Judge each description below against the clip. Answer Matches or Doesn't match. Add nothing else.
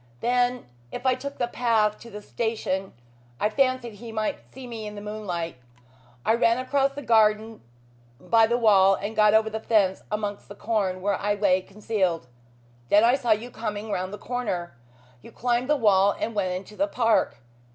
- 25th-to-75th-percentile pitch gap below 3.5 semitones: Matches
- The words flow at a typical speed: Matches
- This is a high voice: Matches